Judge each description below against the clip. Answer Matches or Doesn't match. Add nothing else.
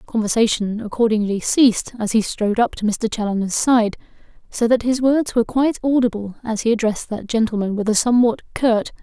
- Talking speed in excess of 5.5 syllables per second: Matches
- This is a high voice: Matches